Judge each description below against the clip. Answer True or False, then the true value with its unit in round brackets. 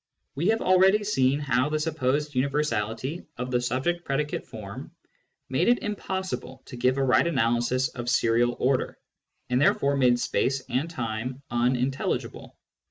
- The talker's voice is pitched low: True (130 Hz)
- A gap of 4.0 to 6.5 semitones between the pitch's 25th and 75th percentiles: False (3.5 semitones)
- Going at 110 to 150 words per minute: True (145 wpm)